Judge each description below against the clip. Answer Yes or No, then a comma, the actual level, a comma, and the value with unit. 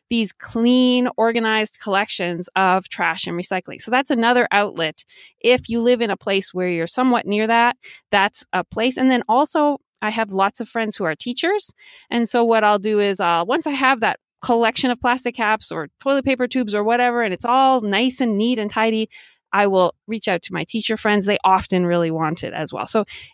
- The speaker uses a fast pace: Yes, fast, 210 wpm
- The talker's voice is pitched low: No, high, 220 Hz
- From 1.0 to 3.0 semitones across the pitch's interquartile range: No, average, 4.1 semitones